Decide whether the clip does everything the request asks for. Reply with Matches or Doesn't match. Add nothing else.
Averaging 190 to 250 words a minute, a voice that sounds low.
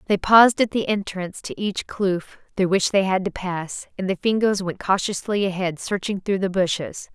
Doesn't match